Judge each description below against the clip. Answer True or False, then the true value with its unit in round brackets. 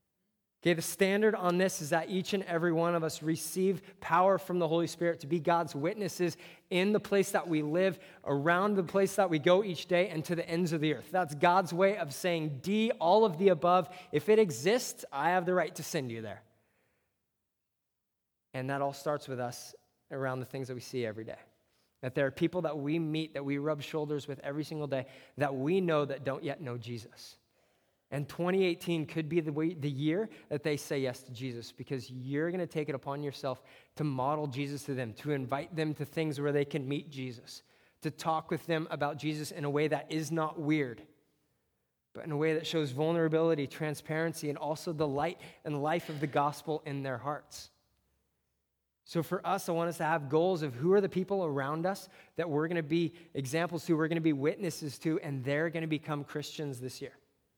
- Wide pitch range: False (3.5 semitones)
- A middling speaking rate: False (220 wpm)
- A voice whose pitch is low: False (155 Hz)